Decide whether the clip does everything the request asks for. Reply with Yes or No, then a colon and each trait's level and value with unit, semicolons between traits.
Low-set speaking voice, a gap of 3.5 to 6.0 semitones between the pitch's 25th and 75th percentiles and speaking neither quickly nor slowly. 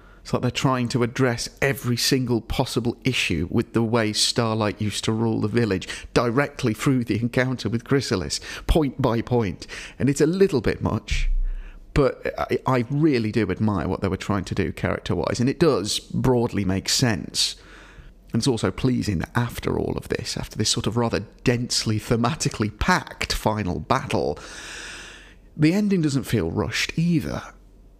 Yes: low, 115 Hz; average, 3.9 semitones; average, 165 wpm